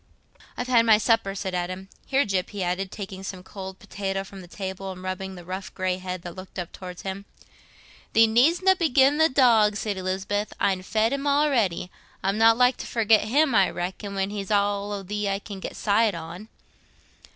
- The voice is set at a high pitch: Yes, high, 200 Hz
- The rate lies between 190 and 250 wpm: Yes, fast, 205 wpm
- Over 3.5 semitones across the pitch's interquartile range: No, average, 3.2 semitones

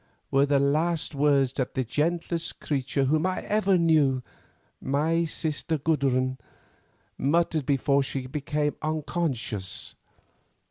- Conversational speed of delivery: No, slow, 110 wpm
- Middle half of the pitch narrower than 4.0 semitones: Yes, average, 3.1 semitones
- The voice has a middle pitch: Yes, medium, 145 Hz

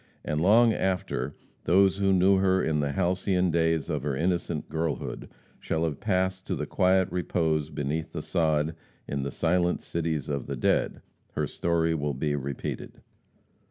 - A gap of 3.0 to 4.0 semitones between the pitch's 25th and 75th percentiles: Yes, average, 3.6 semitones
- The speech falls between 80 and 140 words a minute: No, average, 160 wpm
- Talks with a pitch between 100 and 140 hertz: No, very low, 80 Hz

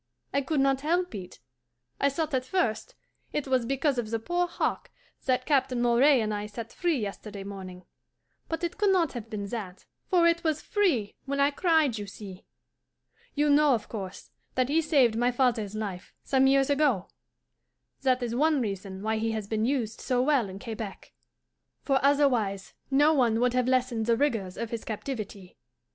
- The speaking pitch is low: No, very high, 250 Hz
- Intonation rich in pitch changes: No, average, 4.9 semitones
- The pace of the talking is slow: No, average, 185 wpm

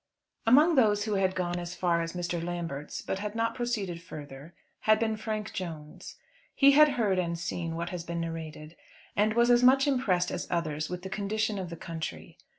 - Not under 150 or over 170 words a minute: No, average, 195 wpm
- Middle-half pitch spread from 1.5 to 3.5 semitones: No, average, 4.5 semitones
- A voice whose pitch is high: No, medium, 180 Hz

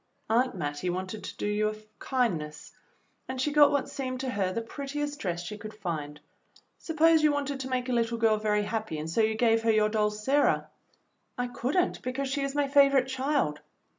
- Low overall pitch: No, high, 230 Hz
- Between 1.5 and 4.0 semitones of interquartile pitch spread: No, average, 4.7 semitones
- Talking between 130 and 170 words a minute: No, fast, 205 wpm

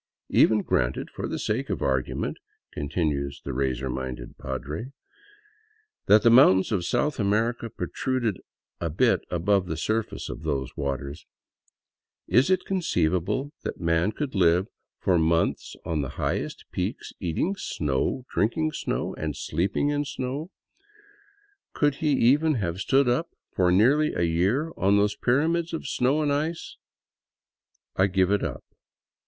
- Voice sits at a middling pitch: No, low, 100 Hz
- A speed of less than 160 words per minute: Yes, average, 150 wpm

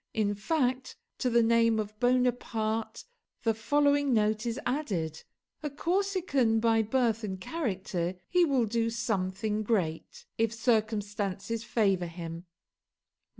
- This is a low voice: No, high, 225 Hz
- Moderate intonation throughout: Yes, average, 3.4 semitones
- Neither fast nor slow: No, slow, 120 wpm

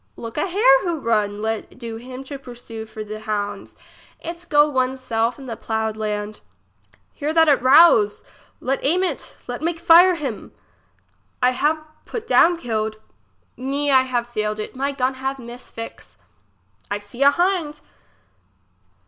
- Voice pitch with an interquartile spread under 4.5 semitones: No, average, 5.2 semitones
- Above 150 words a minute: Yes, average, 160 wpm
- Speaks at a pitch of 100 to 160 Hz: No, very high, 255 Hz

